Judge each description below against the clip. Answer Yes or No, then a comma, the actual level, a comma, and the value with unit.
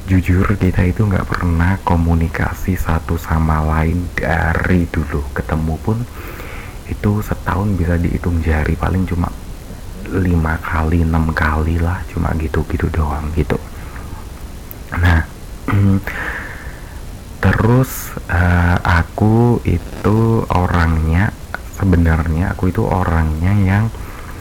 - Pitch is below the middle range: Yes, very low, 85 Hz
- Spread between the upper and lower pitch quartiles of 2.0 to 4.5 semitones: Yes, narrow, 2.6 semitones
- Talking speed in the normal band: Yes, average, 100 wpm